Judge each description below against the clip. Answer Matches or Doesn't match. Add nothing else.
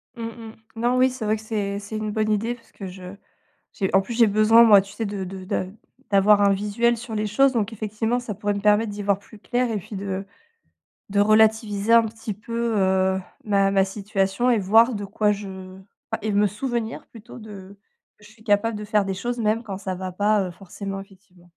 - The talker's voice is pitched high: Matches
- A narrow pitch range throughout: Matches